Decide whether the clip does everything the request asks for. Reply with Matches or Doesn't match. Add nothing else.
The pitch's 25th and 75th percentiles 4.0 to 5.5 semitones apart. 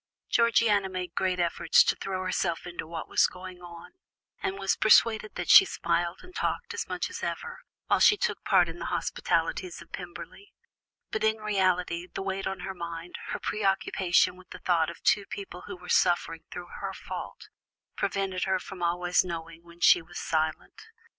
Doesn't match